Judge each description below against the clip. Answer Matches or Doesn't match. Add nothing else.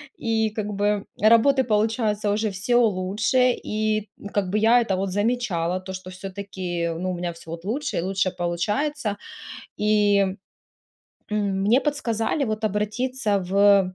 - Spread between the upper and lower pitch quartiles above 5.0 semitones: Doesn't match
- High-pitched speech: Matches